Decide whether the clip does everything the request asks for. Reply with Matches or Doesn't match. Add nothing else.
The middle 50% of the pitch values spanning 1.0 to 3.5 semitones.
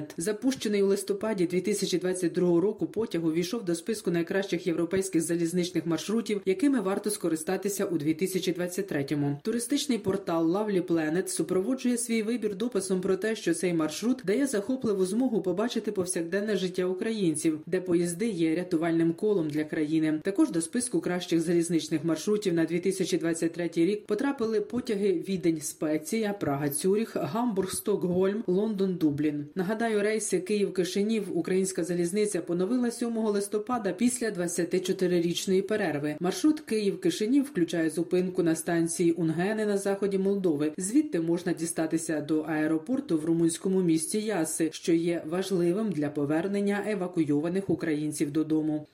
Doesn't match